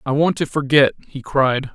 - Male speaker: Yes, male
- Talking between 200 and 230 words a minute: Yes, fast, 205 wpm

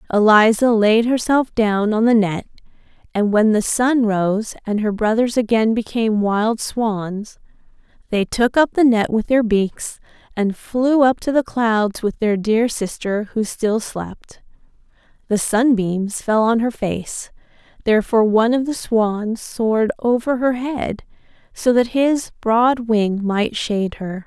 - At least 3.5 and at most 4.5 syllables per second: Yes, 3.9 syllables/s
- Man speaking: No, female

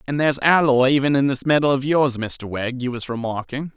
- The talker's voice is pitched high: No, low, 135 Hz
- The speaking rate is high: Yes, fast, 225 wpm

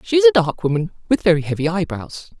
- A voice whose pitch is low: No, medium, 185 Hz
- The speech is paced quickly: Yes, fast, 225 wpm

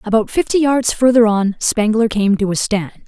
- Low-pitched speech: No, high, 220 Hz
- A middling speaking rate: Yes, average, 195 wpm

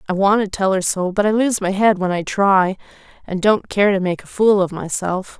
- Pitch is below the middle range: No, high, 195 Hz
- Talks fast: Yes, fast, 255 wpm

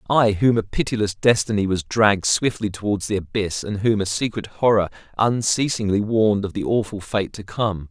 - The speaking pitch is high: No, low, 105 Hz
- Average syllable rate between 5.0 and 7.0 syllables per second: Yes, 5.3 syllables/s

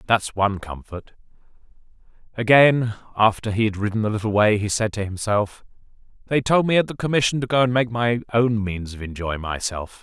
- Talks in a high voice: No, low, 110 Hz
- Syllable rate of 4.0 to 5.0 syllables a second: No, 5.5 syllables/s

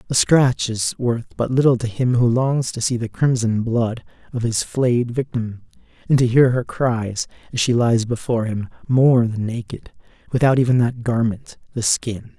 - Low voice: Yes, low, 120 Hz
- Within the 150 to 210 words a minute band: Yes, average, 185 wpm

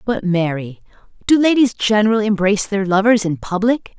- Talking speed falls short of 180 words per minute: Yes, slow, 135 wpm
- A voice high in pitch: Yes, high, 205 Hz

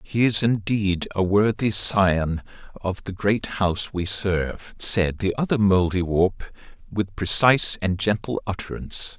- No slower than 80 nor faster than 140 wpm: Yes, slow, 135 wpm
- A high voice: No, low, 100 Hz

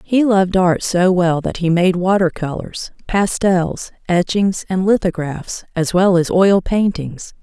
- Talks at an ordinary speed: Yes, average, 155 wpm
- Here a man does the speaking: No, female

